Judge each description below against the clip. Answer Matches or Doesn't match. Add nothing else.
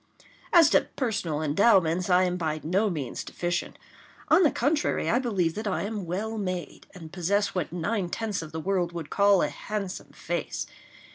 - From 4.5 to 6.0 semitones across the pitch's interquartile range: Doesn't match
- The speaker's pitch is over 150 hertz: Matches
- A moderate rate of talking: Matches